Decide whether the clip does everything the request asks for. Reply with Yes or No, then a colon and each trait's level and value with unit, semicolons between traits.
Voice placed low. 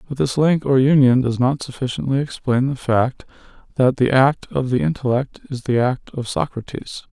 Yes: low, 130 Hz